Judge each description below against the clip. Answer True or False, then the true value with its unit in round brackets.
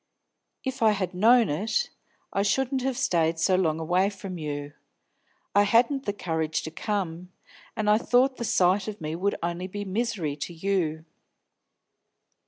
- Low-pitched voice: False (195 Hz)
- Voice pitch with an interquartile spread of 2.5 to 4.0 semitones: False (4.8 semitones)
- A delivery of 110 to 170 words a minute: True (160 wpm)